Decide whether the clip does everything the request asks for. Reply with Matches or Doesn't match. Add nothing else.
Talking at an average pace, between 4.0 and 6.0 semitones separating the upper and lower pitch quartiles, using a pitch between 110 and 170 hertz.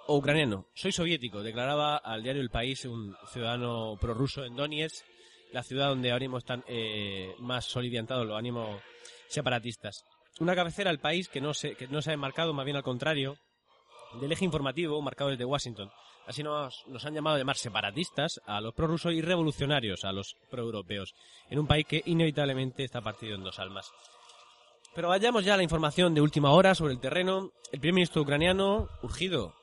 Matches